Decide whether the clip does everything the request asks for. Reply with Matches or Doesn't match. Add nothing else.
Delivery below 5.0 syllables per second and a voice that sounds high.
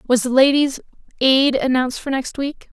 Matches